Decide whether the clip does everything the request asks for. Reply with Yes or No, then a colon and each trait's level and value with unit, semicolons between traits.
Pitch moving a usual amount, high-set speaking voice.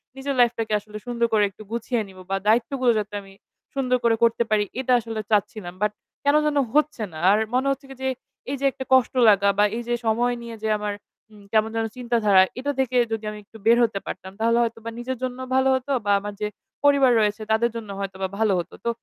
Yes: average, 3.2 semitones; high, 230 Hz